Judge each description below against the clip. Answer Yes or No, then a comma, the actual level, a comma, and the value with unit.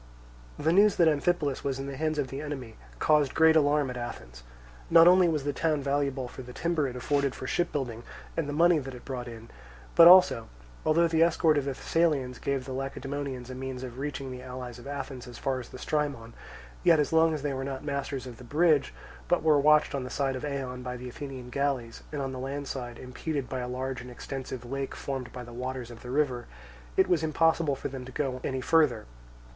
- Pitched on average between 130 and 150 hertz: Yes, low, 135 Hz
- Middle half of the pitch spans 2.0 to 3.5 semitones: Yes, average, 3.0 semitones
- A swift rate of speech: Yes, fast, 225 wpm